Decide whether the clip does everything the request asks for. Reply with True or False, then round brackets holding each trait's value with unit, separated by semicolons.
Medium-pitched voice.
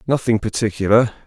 False (110 Hz)